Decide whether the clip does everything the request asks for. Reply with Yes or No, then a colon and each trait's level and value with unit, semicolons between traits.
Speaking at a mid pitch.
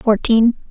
No: high, 225 Hz